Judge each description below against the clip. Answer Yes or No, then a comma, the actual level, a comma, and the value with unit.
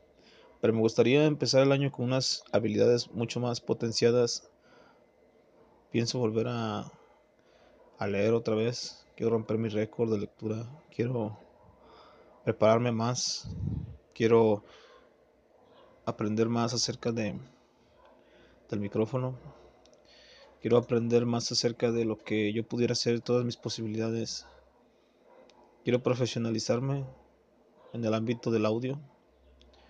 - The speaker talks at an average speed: No, slow, 110 wpm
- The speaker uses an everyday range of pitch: No, narrow, 1.7 semitones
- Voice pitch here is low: Yes, low, 115 Hz